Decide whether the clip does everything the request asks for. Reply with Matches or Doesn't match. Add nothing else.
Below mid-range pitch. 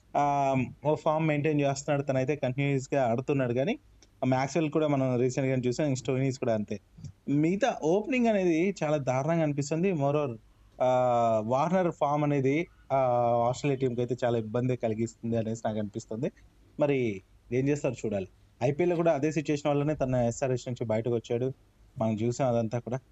Matches